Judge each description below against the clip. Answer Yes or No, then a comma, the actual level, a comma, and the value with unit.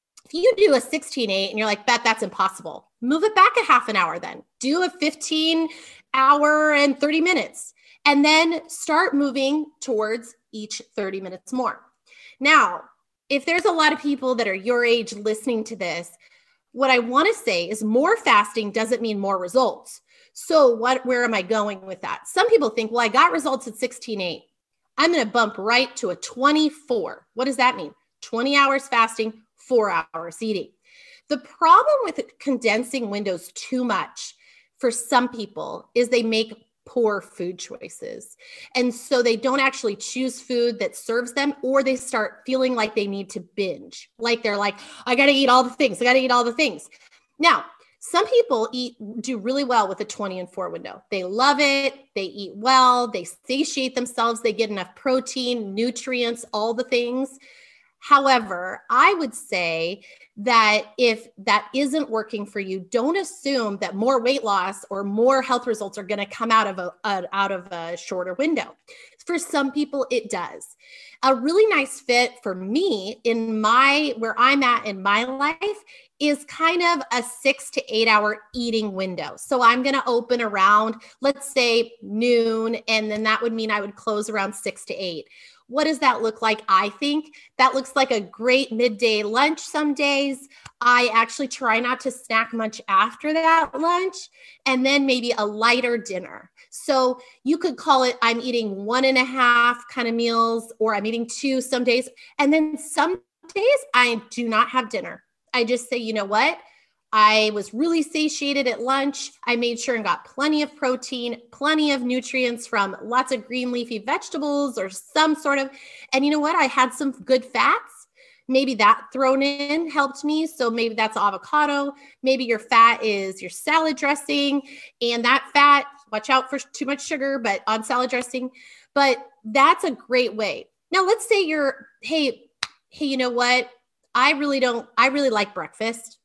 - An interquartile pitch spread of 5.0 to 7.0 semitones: No, average, 4.2 semitones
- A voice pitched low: No, very high, 250 Hz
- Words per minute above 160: Yes, average, 185 wpm